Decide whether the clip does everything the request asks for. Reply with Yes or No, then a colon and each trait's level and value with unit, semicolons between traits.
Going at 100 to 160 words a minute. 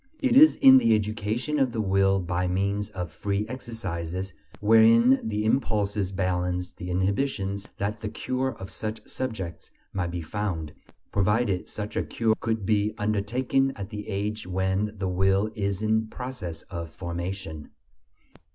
Yes: average, 150 wpm